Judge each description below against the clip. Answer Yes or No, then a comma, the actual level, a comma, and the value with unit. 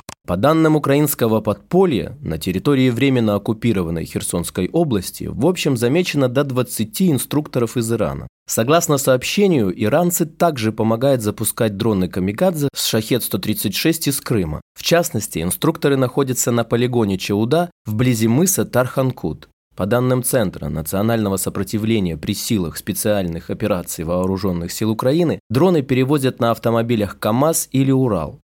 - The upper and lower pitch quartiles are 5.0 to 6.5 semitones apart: Yes, average, 5.3 semitones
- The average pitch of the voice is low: Yes, low, 120 Hz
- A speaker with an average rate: Yes, average, 125 wpm